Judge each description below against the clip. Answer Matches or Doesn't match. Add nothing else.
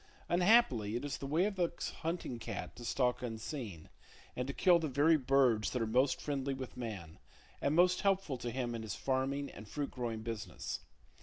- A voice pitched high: Doesn't match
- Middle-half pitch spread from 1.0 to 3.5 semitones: Doesn't match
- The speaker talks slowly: Doesn't match